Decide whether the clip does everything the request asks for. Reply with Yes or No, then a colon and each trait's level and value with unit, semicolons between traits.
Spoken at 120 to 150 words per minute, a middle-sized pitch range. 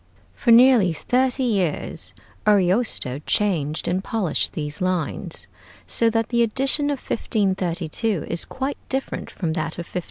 No: slow, 135 wpm; wide, 5.9 semitones